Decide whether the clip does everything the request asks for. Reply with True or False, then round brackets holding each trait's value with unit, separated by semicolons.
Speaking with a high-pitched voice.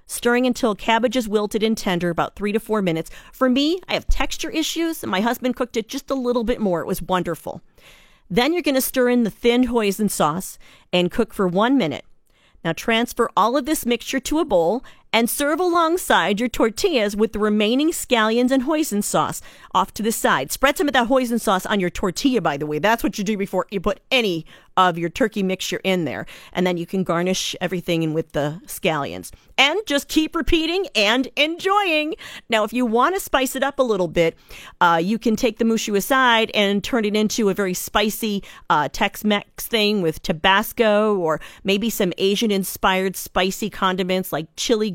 True (220 Hz)